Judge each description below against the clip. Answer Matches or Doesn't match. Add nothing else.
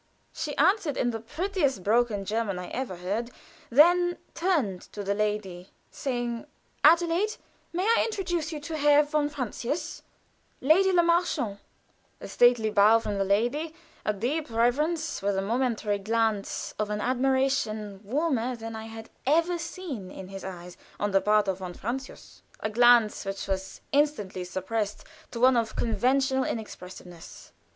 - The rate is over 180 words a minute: Doesn't match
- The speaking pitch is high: Matches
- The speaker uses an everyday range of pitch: Doesn't match